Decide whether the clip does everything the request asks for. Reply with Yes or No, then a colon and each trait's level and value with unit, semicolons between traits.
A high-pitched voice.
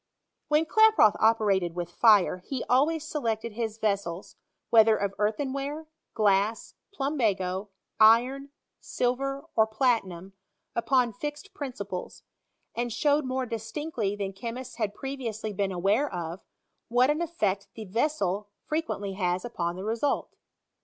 Yes: high, 225 Hz